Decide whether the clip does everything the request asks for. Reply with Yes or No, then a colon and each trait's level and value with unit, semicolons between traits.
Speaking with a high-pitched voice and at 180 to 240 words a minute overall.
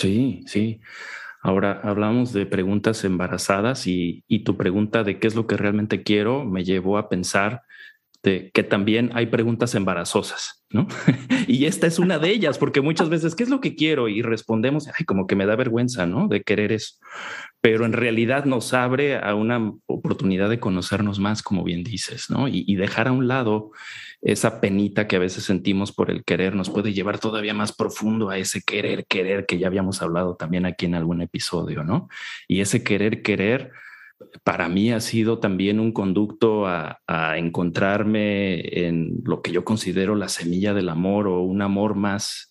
No: low, 105 Hz; average, 185 wpm